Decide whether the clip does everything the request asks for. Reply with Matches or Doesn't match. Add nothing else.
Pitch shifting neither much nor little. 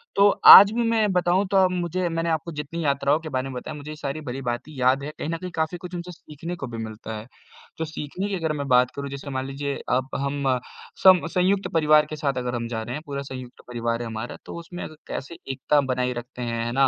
Matches